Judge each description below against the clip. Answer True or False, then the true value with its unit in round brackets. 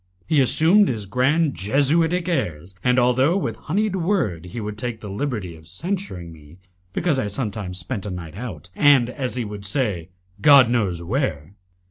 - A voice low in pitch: True (120 Hz)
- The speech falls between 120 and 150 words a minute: False (170 wpm)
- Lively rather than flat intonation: True (7.8 semitones)